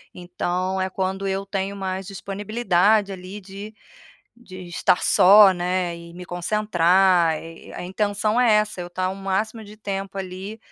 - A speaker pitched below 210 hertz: Yes, high, 190 Hz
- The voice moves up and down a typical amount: No, narrow, 2.1 semitones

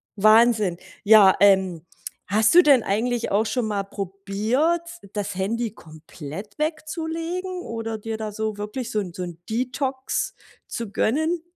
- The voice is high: Yes, high, 220 Hz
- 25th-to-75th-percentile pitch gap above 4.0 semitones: Yes, average, 4.9 semitones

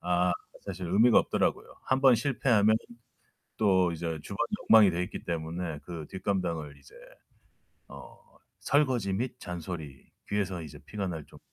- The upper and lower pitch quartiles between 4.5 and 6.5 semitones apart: No, average, 4.0 semitones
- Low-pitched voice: Yes, very low, 90 Hz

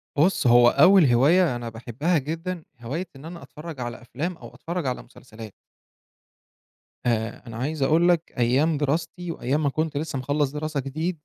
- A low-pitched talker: No, medium, 145 Hz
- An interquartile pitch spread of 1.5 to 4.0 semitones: No, average, 4.8 semitones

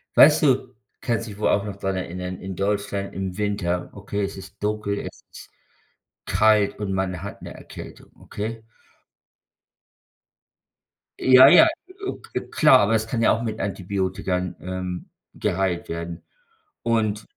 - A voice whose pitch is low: Yes, low, 100 Hz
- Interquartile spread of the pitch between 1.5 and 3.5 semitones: Yes, average, 2.8 semitones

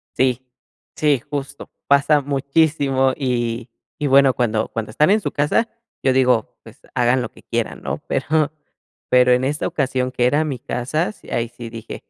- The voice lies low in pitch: Yes, low, 130 Hz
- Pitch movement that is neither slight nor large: Yes, average, 3.0 semitones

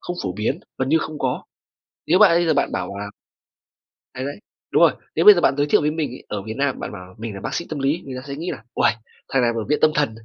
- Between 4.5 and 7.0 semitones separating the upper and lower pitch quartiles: Yes, wide, 5.6 semitones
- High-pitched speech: No, medium, 140 Hz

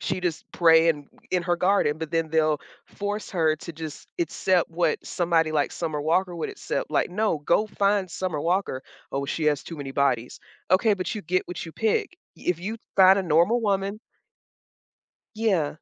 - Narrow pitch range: No, average, 3.7 semitones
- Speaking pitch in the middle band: Yes, medium, 170 Hz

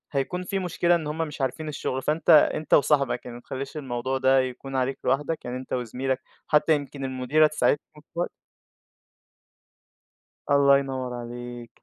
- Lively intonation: No, average, 2.9 semitones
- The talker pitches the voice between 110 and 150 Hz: Yes, low, 135 Hz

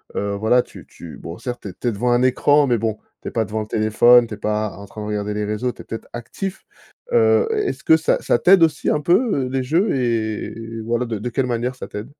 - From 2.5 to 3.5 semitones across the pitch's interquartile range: No, average, 3.9 semitones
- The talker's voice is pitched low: Yes, low, 120 Hz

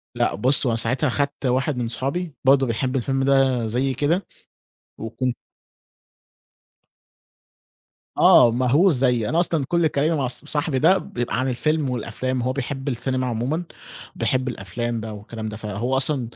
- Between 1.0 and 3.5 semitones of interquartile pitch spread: Yes, average, 3.0 semitones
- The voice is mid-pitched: No, low, 130 Hz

